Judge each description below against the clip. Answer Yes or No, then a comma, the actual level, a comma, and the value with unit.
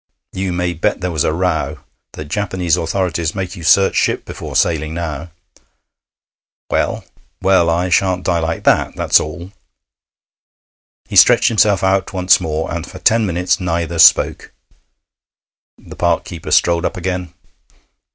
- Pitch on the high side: No, very low, 90 Hz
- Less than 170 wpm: Yes, average, 145 wpm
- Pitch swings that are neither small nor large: No, narrow, 2.1 semitones